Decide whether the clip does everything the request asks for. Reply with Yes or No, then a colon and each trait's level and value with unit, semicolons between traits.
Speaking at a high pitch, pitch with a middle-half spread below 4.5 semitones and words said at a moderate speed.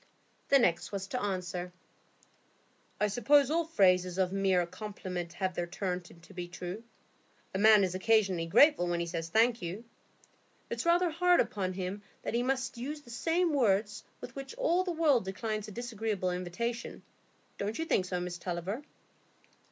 No: high, 200 Hz; wide, 5.5 semitones; average, 165 wpm